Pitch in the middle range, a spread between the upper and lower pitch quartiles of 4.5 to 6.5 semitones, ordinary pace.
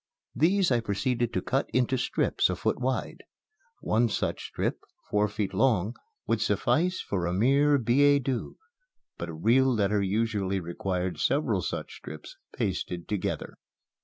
No: low, 115 Hz; average, 5.2 semitones; average, 145 wpm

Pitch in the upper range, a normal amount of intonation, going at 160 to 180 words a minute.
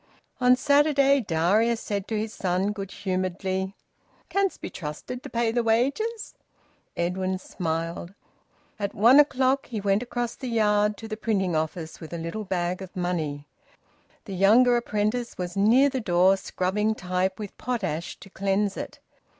No: high, 205 Hz; average, 4.4 semitones; average, 150 wpm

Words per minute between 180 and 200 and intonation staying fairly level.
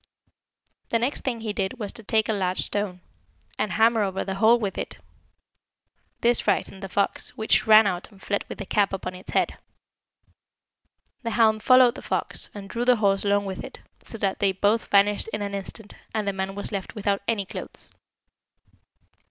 Yes: average, 190 wpm; narrow, 2.2 semitones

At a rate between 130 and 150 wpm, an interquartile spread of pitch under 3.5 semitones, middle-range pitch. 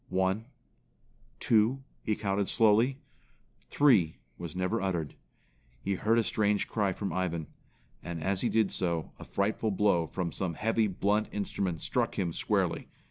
No: average, 145 wpm; average, 3.1 semitones; low, 100 Hz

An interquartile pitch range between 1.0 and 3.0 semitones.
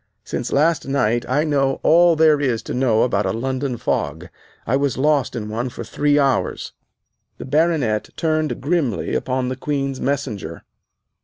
No: average, 3.5 semitones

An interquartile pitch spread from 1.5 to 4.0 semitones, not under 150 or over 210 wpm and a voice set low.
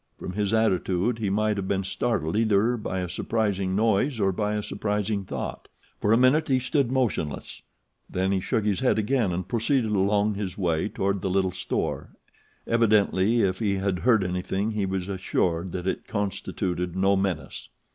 Yes: average, 2.9 semitones; average, 175 wpm; low, 100 Hz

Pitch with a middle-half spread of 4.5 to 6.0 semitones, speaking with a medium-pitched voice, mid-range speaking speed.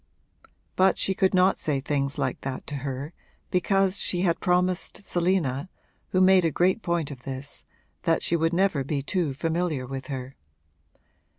Yes: average, 5.0 semitones; medium, 165 Hz; average, 165 wpm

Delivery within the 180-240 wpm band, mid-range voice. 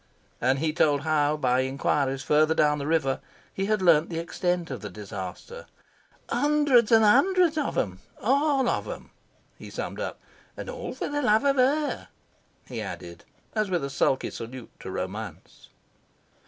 No: average, 165 wpm; medium, 160 Hz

